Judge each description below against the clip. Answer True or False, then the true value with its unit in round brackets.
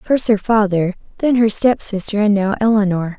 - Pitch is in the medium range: False (210 Hz)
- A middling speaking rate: True (190 wpm)